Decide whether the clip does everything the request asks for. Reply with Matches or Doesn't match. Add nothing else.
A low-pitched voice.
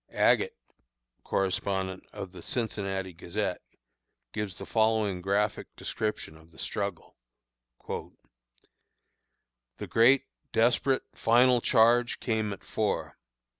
Matches